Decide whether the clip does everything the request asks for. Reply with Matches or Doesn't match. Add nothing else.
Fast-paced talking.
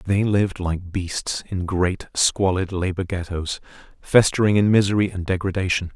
Doesn't match